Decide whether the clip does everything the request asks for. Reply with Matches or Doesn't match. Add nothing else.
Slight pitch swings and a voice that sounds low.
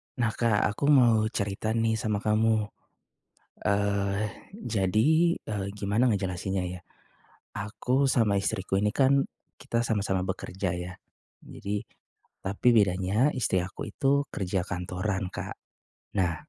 Doesn't match